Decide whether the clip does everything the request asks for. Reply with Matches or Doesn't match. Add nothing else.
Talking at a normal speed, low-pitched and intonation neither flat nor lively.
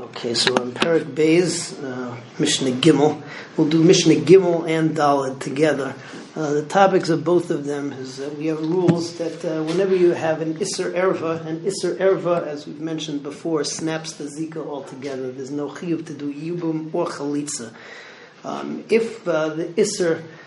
Doesn't match